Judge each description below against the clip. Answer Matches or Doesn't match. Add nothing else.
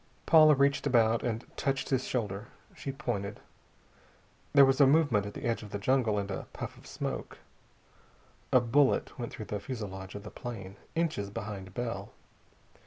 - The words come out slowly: Doesn't match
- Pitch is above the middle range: Doesn't match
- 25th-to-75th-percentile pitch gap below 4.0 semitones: Doesn't match